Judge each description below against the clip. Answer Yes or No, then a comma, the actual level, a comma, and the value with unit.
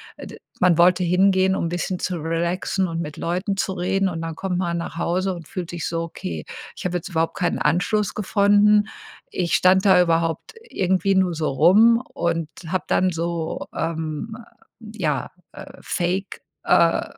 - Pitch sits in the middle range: Yes, medium, 180 Hz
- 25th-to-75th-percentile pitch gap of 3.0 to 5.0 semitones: No, narrow, 2.4 semitones